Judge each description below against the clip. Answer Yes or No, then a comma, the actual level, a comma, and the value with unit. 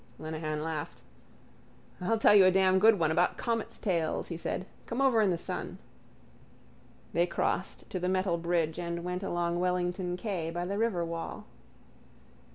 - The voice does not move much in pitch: Yes, narrow, 2.1 semitones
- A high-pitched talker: No, medium, 180 Hz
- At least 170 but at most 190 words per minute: No, average, 160 wpm